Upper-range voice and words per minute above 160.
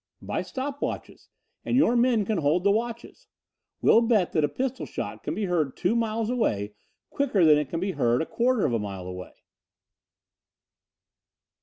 Yes: high, 200 Hz; average, 175 wpm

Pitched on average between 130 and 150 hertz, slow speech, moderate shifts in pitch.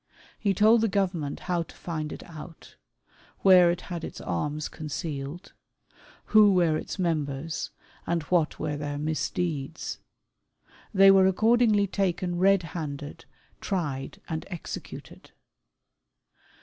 No: medium, 170 Hz; slow, 120 wpm; average, 4.0 semitones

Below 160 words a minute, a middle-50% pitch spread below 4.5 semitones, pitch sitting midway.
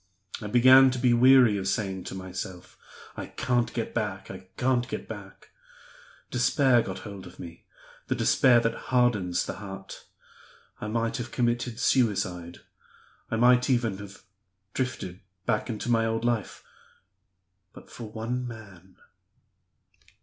No: average, 140 wpm; average, 4.1 semitones; low, 115 Hz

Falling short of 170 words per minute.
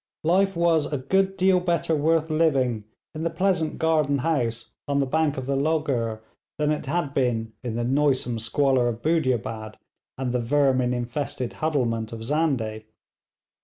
Yes: average, 160 wpm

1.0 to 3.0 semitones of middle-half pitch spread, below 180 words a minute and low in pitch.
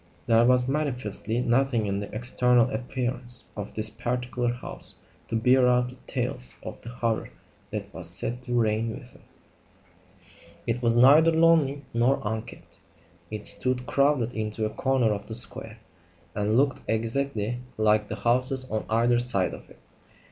Yes: narrow, 2.5 semitones; average, 155 wpm; low, 120 Hz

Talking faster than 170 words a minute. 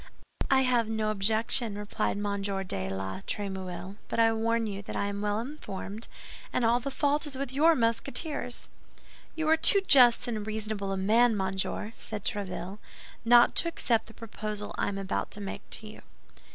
Yes: average, 180 wpm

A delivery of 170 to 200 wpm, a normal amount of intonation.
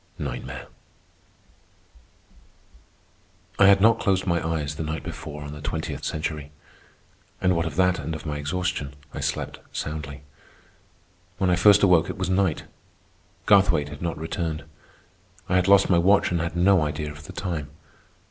No: average, 155 wpm; average, 3.6 semitones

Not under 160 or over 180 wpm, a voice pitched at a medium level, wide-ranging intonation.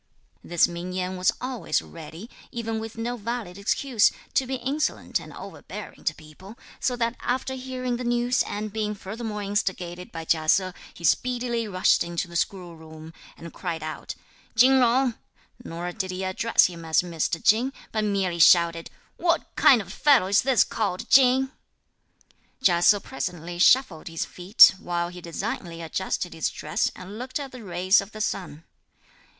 No: average, 165 wpm; high, 195 Hz; wide, 5.7 semitones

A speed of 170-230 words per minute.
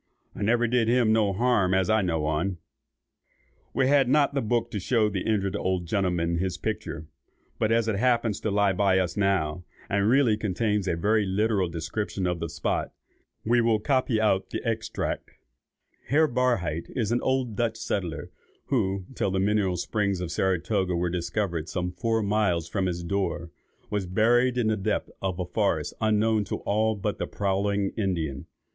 Yes: average, 175 wpm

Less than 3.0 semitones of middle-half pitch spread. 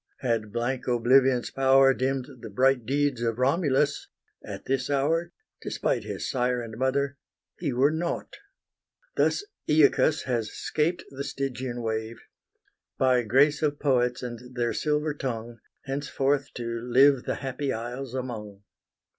Yes: narrow, 2.6 semitones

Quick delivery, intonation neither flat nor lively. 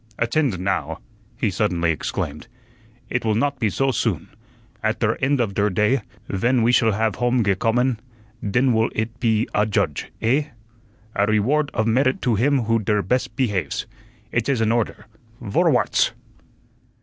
No: average, 155 wpm; average, 3.4 semitones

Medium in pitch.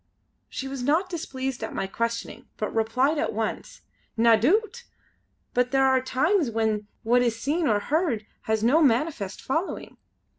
No: very high, 255 Hz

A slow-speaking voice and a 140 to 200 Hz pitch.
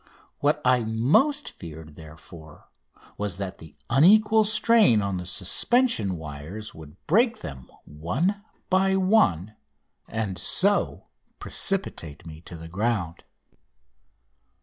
No: slow, 110 wpm; low, 105 Hz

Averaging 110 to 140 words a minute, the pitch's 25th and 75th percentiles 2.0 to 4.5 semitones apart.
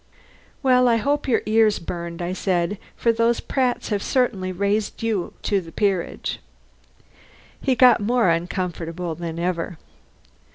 No: slow, 135 wpm; average, 5.0 semitones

